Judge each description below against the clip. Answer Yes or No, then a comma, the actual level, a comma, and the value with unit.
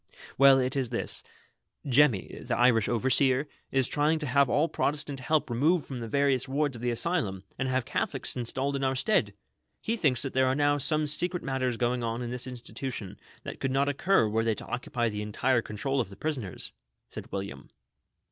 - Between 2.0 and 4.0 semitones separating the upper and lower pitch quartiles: Yes, average, 3.2 semitones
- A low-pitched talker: Yes, low, 130 Hz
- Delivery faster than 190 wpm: Yes, average, 200 wpm